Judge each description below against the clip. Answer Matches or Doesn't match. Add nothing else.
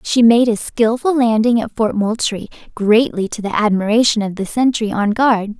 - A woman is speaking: Matches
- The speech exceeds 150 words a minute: Matches